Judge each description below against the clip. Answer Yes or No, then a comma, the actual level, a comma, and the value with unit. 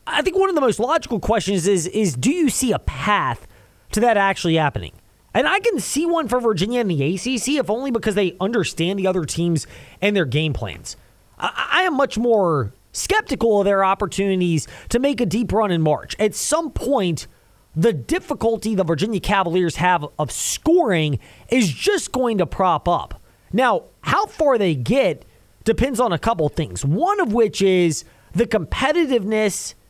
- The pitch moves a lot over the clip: Yes, wide, 6.1 semitones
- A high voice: Yes, high, 205 Hz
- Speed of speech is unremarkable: Yes, average, 180 wpm